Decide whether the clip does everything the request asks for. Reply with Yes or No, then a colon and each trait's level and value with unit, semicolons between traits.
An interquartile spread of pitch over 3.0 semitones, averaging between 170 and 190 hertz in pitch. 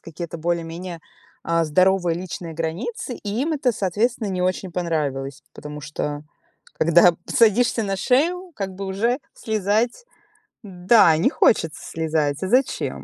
Yes: average, 5.1 semitones; medium, 185 Hz